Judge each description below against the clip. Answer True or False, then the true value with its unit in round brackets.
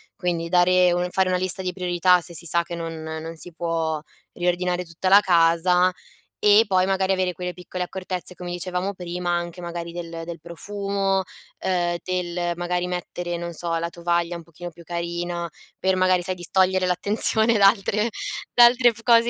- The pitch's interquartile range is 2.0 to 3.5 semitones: False (1.4 semitones)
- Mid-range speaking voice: True (180 Hz)